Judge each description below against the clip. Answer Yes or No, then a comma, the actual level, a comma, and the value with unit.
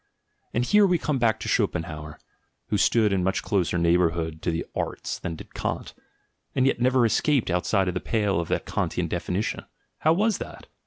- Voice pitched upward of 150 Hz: No, low, 100 Hz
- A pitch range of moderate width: No, wide, 6.7 semitones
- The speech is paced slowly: No, average, 180 wpm